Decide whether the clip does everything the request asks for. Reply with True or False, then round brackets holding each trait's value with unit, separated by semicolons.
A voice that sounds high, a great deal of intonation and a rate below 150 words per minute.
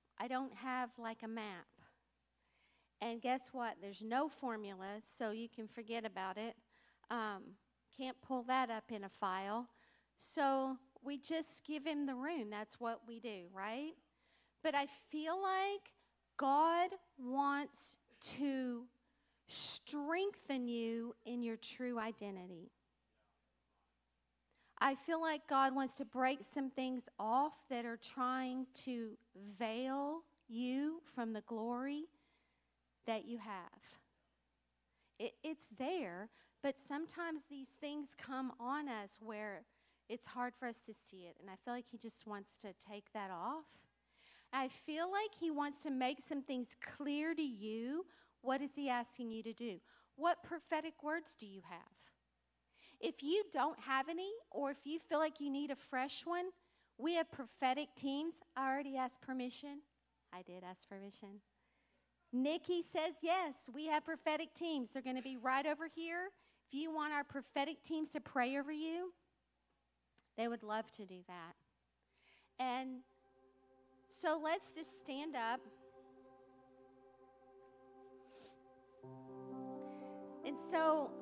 True (255 Hz; 5.7 semitones; 140 wpm)